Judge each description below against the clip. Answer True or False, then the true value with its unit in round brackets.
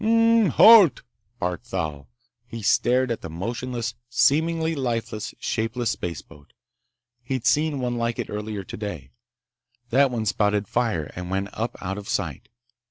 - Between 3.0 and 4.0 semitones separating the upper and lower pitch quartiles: False (4.6 semitones)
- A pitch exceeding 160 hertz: False (115 Hz)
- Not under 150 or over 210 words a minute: False (140 wpm)